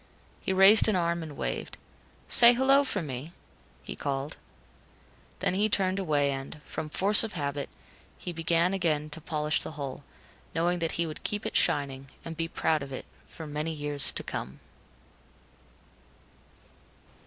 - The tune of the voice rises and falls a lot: No, average, 4.2 semitones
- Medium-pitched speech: Yes, medium, 160 Hz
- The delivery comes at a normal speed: Yes, average, 155 wpm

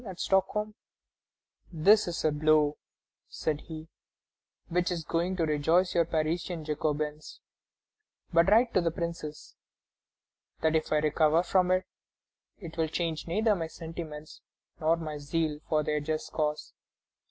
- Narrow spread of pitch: Yes, narrow, 2.2 semitones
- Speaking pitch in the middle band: Yes, medium, 160 Hz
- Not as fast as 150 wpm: Yes, average, 140 wpm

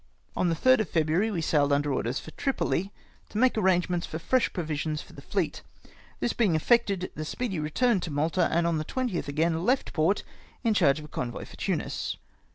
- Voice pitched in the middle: Yes, medium, 170 Hz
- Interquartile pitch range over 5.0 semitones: Yes, wide, 5.4 semitones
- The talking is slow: No, average, 200 wpm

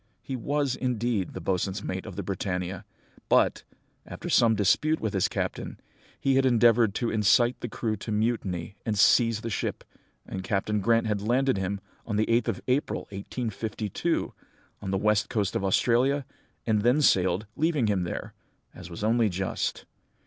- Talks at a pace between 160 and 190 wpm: Yes, average, 170 wpm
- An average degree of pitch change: Yes, average, 3.6 semitones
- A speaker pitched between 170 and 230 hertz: No, low, 110 Hz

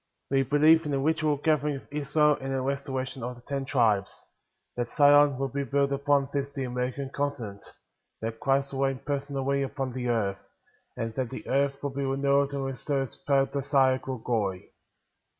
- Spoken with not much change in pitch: Yes, narrow, 1.6 semitones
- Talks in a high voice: No, low, 135 Hz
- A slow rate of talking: No, average, 185 wpm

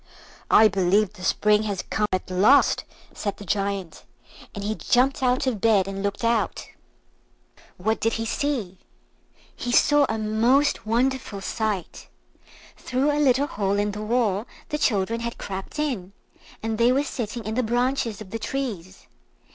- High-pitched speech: Yes, high, 220 Hz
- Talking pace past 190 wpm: No, average, 160 wpm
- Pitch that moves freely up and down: No, average, 3.8 semitones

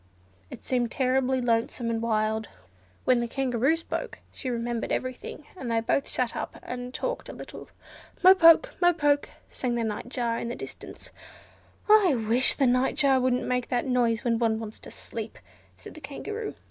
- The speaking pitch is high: Yes, very high, 250 Hz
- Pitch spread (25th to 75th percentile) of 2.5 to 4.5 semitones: Yes, average, 2.9 semitones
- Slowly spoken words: No, average, 175 wpm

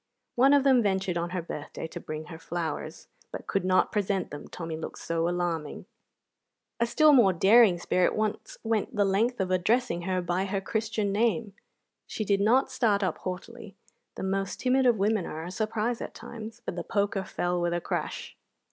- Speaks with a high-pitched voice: Yes, high, 195 Hz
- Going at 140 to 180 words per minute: No, average, 190 wpm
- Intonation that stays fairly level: No, average, 4.2 semitones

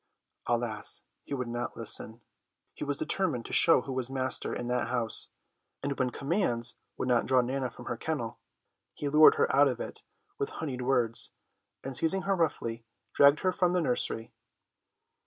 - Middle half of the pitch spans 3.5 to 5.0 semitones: No, average, 2.9 semitones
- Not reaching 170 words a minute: No, average, 175 wpm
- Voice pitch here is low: Yes, low, 130 Hz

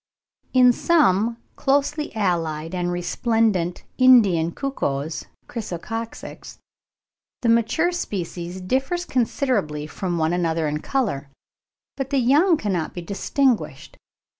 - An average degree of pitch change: No, wide, 7.1 semitones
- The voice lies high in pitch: Yes, high, 205 Hz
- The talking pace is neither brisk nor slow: No, slow, 105 wpm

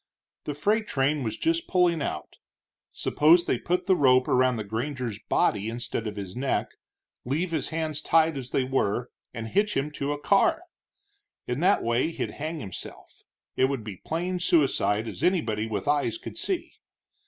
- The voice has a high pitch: No, medium, 145 Hz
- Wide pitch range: Yes, wide, 6.3 semitones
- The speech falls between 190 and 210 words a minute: No, average, 175 wpm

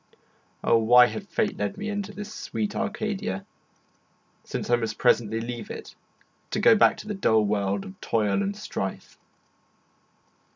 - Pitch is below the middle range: No, high, 190 Hz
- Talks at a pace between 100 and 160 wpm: Yes, average, 155 wpm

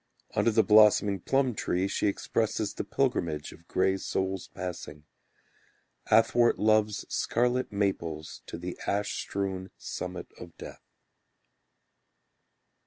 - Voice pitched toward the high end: No, low, 100 Hz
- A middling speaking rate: No, slow, 110 wpm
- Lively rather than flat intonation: No, average, 3.2 semitones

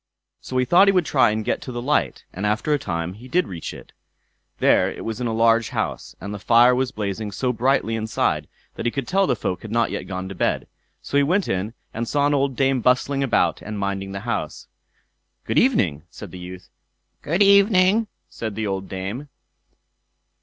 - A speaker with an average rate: No, fast, 210 wpm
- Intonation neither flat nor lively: No, wide, 5.7 semitones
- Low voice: Yes, low, 115 Hz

